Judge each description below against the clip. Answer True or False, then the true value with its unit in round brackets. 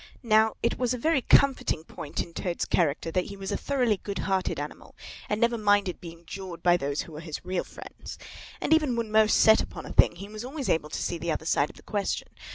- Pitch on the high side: True (200 Hz)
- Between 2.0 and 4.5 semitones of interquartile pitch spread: False (5.4 semitones)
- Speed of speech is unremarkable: False (240 wpm)